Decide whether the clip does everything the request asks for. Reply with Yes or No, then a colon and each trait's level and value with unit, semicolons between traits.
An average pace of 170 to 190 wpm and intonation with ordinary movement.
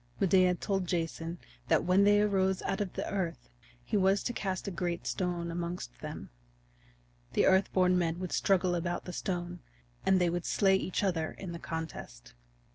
No: average, 180 wpm; narrow, 2.0 semitones